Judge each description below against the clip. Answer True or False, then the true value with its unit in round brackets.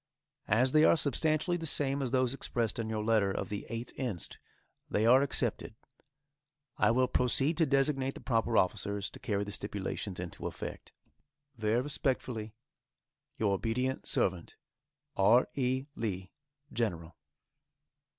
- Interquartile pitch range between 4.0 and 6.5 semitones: True (4.3 semitones)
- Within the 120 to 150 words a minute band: True (140 wpm)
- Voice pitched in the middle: False (115 Hz)